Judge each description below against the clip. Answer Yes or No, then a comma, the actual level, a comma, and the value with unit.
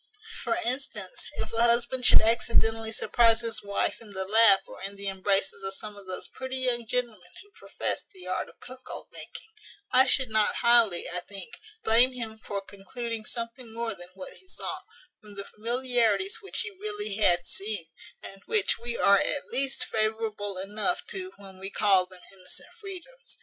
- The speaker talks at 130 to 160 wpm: No, average, 180 wpm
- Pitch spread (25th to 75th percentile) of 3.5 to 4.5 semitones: Yes, average, 4.1 semitones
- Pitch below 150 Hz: No, high, 225 Hz